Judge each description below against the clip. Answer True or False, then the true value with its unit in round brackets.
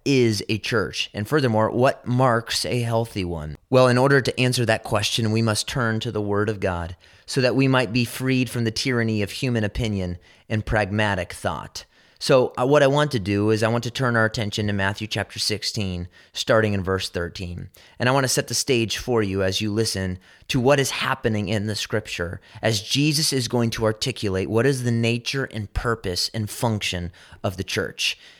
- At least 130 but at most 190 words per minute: False (205 wpm)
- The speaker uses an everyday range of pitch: True (3.5 semitones)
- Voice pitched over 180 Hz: False (110 Hz)